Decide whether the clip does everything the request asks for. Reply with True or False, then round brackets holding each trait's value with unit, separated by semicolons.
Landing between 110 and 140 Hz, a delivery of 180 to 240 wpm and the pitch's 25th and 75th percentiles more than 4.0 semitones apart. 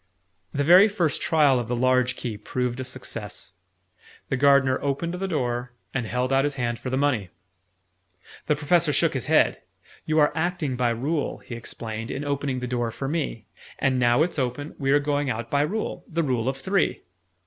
False (135 Hz; 190 wpm; 3.3 semitones)